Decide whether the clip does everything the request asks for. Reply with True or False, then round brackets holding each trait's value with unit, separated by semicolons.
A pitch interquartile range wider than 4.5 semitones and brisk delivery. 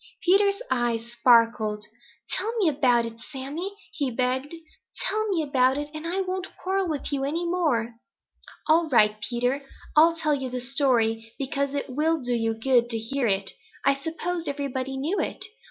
False (5.2 semitones; 170 wpm)